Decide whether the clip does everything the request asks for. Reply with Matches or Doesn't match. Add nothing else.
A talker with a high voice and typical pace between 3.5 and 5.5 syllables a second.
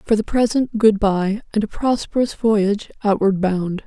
Matches